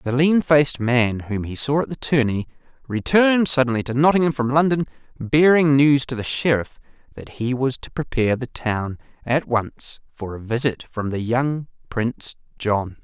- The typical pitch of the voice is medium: No, low, 130 Hz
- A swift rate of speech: No, average, 175 wpm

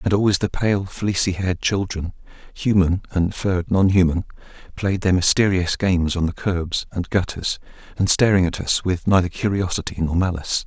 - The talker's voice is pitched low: Yes, very low, 95 Hz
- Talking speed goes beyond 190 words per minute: No, average, 165 wpm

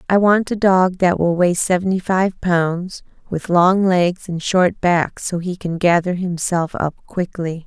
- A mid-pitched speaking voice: Yes, medium, 180 Hz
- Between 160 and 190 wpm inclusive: Yes, average, 180 wpm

